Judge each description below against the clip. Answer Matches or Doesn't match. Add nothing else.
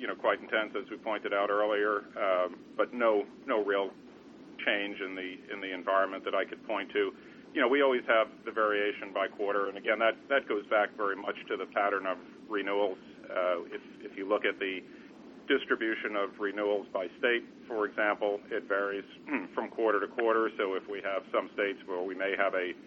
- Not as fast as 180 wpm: Doesn't match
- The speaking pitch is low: Matches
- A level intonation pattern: Matches